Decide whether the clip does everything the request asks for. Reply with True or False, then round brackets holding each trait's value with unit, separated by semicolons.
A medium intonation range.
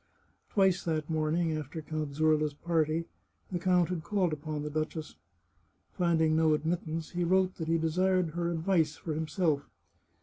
False (2.1 semitones)